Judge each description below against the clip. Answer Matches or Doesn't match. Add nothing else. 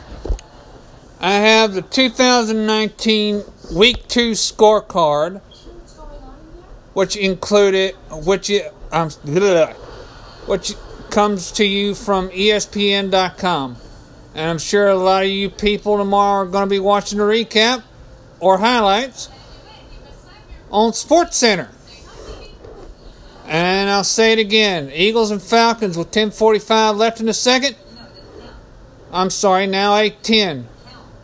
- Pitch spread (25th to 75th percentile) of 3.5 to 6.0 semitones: Doesn't match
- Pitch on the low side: Doesn't match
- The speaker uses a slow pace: Matches